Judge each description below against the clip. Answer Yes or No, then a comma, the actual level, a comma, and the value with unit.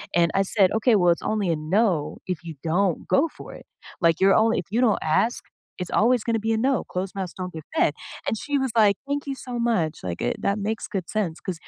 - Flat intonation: No, average, 4.2 semitones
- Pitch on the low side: No, high, 200 Hz